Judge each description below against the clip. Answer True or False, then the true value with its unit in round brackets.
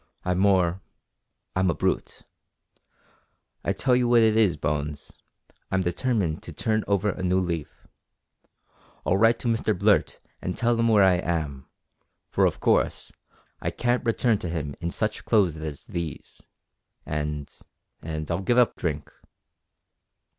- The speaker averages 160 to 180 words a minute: False (145 wpm)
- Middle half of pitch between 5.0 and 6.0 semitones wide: True (5.3 semitones)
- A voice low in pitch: True (95 Hz)